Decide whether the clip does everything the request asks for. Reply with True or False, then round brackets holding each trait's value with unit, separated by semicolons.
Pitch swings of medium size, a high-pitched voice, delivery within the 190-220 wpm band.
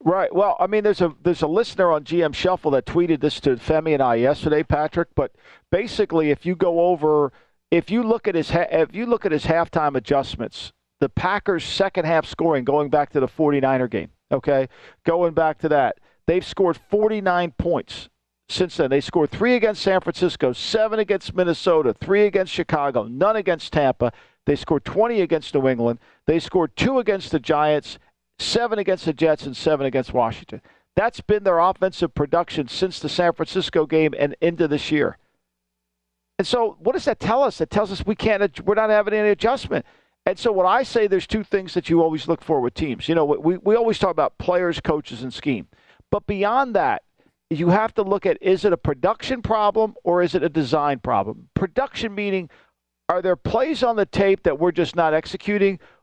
False (5.0 semitones; 170 Hz; 200 wpm)